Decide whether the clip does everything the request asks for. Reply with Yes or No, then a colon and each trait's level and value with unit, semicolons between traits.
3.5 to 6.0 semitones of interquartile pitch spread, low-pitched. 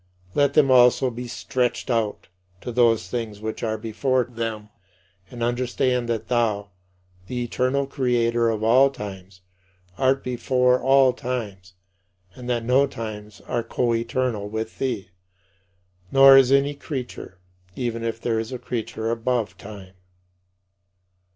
No: narrow, 2.4 semitones; low, 120 Hz